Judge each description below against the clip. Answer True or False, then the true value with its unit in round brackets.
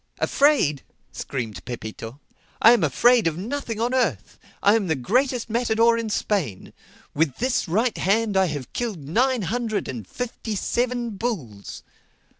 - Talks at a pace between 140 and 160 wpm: True (145 wpm)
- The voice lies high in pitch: True (215 Hz)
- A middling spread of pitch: False (8.2 semitones)